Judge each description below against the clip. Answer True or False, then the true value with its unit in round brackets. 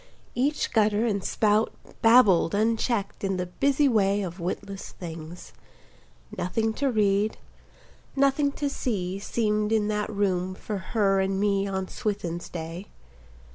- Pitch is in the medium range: False (205 Hz)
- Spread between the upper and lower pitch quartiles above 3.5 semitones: False (2.8 semitones)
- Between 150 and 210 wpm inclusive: False (135 wpm)